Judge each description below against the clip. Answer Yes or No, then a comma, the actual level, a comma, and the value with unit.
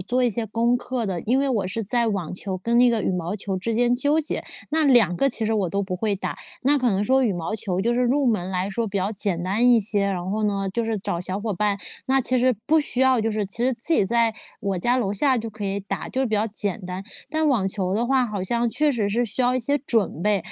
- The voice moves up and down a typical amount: Yes, average, 3.9 semitones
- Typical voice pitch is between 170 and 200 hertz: No, high, 220 Hz